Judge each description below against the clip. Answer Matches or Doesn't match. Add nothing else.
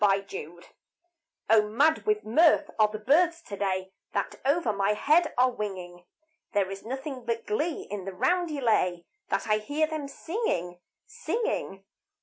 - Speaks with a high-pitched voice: Matches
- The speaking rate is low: Doesn't match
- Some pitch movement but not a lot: Doesn't match